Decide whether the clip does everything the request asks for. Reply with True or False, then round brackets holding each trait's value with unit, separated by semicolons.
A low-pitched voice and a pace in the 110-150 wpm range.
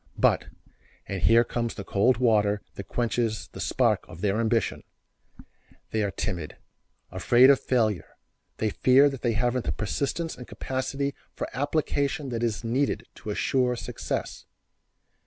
True (120 Hz; 145 wpm)